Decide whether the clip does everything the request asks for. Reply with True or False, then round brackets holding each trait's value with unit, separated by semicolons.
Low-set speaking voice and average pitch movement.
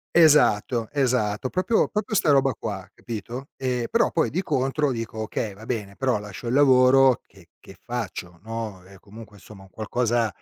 True (120 Hz; 4.1 semitones)